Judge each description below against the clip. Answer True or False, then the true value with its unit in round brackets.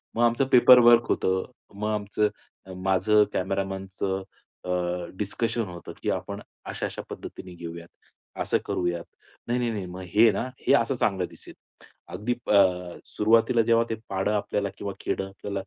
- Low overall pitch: True (100 Hz)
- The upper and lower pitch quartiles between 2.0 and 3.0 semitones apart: False (3.4 semitones)